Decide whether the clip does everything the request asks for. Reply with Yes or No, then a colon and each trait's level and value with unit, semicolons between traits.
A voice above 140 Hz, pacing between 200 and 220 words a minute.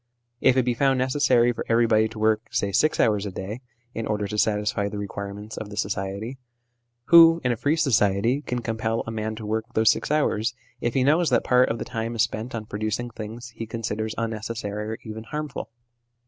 No: low, 110 Hz; fast, 205 wpm